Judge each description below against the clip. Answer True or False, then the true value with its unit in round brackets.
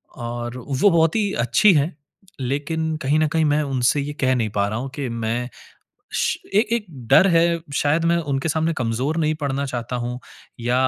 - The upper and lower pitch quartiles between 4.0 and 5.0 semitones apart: True (4.6 semitones)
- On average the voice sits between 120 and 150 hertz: True (140 Hz)